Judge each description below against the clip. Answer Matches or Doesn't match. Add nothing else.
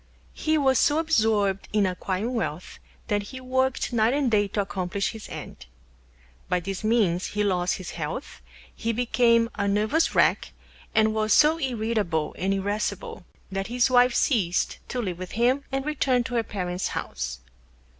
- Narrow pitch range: Doesn't match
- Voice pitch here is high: Matches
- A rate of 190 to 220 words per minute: Doesn't match